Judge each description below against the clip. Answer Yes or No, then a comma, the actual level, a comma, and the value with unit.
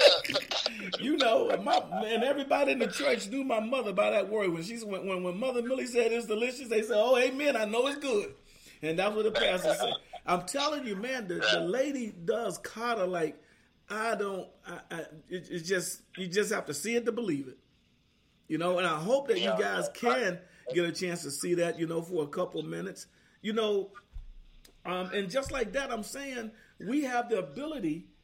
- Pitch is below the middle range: No, high, 215 Hz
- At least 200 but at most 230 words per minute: Yes, fast, 205 wpm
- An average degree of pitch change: No, wide, 5.9 semitones